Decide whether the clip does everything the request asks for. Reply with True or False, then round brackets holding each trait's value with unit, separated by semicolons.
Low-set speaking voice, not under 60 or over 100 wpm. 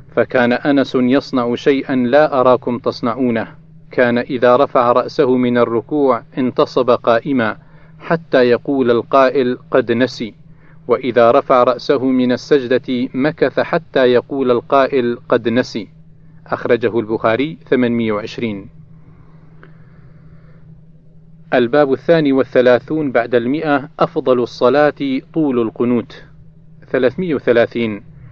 True (130 Hz; 95 wpm)